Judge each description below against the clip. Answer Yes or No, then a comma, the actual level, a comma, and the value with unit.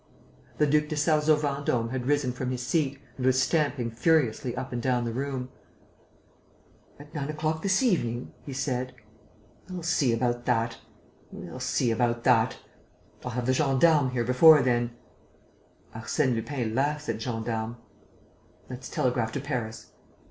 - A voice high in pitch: No, low, 130 Hz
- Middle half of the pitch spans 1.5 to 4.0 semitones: Yes, average, 3.6 semitones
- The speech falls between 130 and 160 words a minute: Yes, average, 150 wpm